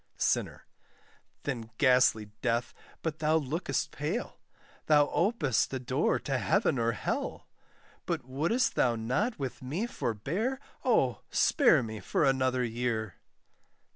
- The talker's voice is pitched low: Yes, low, 130 Hz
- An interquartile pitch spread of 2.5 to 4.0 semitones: No, average, 5.2 semitones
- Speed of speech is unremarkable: No, slow, 125 wpm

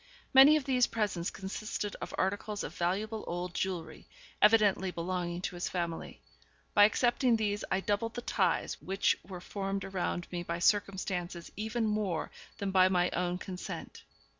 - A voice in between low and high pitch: No, high, 195 Hz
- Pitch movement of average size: Yes, average, 3.1 semitones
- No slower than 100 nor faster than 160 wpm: Yes, average, 155 wpm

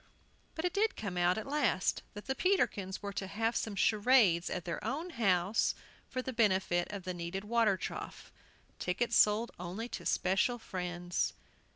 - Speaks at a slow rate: No, average, 170 wpm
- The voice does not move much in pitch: No, average, 4.7 semitones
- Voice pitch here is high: Yes, high, 205 Hz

